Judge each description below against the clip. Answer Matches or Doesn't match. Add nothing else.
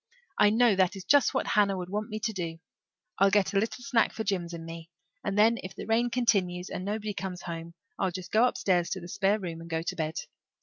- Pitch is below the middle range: Doesn't match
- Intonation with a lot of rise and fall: Doesn't match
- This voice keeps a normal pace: Doesn't match